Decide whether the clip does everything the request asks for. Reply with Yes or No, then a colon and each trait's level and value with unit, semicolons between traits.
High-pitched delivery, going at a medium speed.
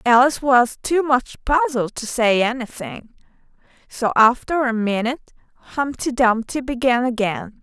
No: high, 245 Hz; slow, 125 wpm